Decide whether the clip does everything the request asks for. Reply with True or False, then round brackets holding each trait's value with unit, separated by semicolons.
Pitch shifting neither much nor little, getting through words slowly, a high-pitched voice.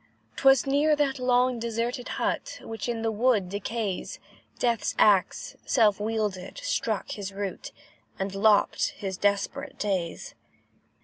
True (3.6 semitones; 125 wpm; 220 Hz)